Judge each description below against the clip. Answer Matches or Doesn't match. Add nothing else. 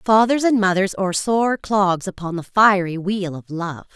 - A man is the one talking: Doesn't match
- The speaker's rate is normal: Matches